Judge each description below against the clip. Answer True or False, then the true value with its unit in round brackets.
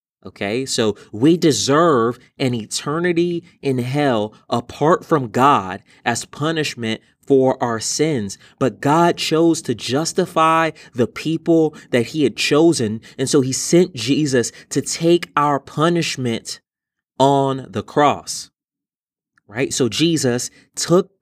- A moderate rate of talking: False (120 wpm)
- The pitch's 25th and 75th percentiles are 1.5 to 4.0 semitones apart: False (4.7 semitones)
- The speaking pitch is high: False (140 Hz)